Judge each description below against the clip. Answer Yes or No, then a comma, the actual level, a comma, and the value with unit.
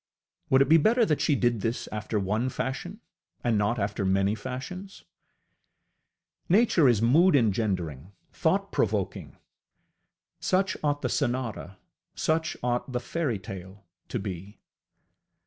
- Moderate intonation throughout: No, wide, 6.6 semitones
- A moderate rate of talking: No, slow, 125 wpm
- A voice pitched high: No, low, 120 Hz